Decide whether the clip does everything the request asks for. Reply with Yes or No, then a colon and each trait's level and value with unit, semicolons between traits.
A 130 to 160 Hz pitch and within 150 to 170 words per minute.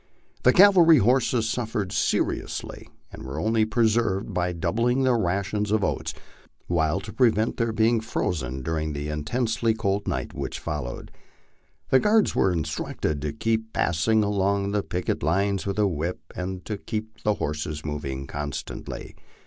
No: low, 100 Hz; average, 155 wpm